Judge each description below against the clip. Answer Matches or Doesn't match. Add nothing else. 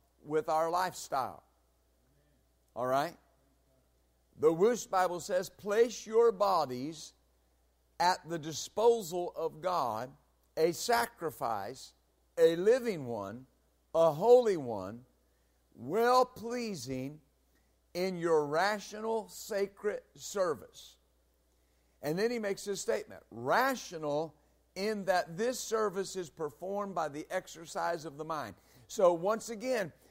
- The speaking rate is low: Matches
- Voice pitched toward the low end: Doesn't match